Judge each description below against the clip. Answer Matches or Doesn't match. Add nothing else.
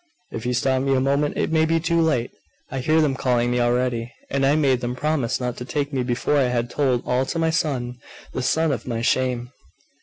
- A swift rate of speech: Matches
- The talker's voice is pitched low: Matches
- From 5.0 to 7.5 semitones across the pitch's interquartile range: Doesn't match